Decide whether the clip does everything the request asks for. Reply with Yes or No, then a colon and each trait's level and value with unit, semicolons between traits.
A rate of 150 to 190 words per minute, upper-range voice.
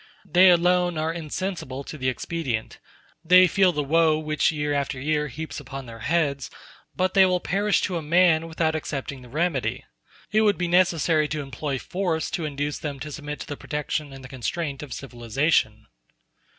No: average, 180 wpm; medium, 155 Hz